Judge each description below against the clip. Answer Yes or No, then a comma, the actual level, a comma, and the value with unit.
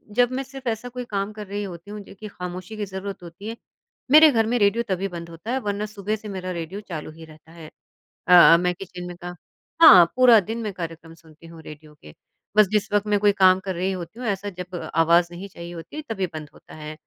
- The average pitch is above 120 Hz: Yes, high, 190 Hz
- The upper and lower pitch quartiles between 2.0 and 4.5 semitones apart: Yes, average, 3.8 semitones